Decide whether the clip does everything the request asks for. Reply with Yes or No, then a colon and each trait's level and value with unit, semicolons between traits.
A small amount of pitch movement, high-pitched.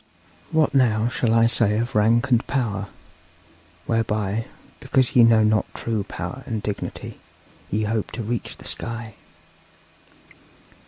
No: narrow, 1.9 semitones; low, 115 Hz